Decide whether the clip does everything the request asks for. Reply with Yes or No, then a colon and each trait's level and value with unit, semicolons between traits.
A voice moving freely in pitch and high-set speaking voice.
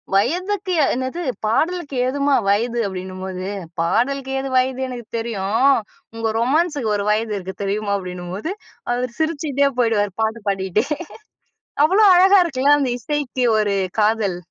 Yes: wide, 5.8 semitones; high, 240 Hz